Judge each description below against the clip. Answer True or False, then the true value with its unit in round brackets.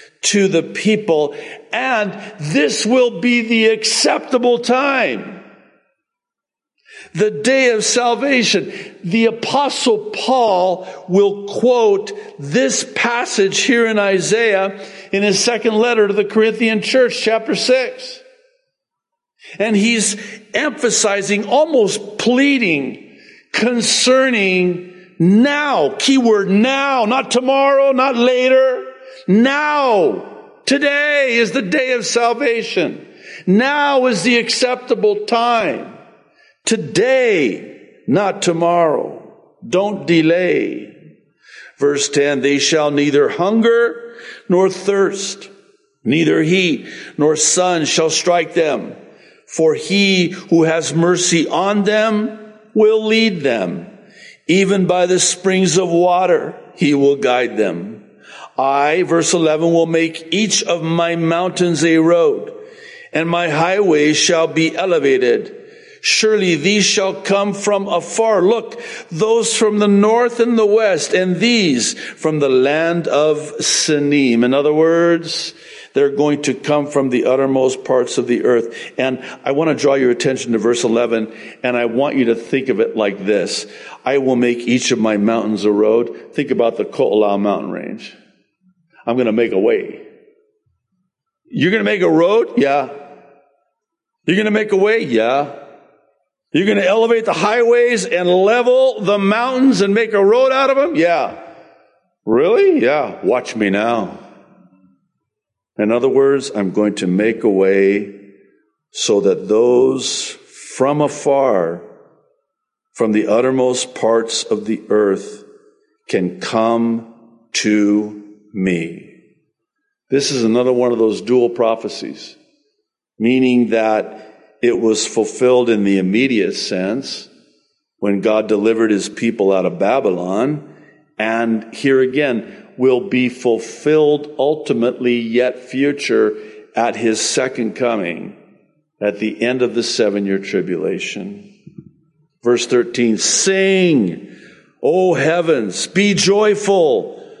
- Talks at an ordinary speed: False (125 wpm)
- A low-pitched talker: False (185 Hz)